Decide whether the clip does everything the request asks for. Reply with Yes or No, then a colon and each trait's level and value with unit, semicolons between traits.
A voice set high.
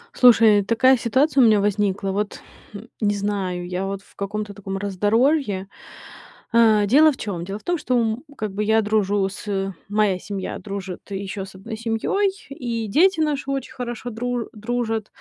Yes: high, 215 Hz